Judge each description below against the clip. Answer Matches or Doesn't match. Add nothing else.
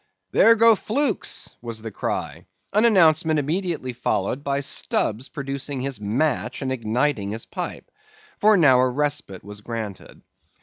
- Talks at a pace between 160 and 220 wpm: Doesn't match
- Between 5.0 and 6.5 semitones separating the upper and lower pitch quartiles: Matches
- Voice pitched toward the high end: Doesn't match